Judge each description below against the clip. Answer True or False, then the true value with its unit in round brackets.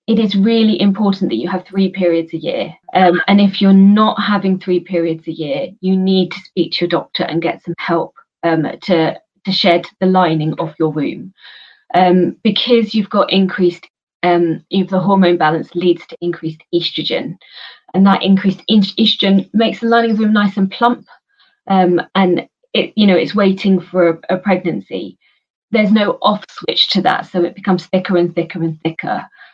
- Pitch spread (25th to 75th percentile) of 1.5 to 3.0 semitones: True (2.5 semitones)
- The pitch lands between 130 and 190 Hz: True (185 Hz)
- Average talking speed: False (190 wpm)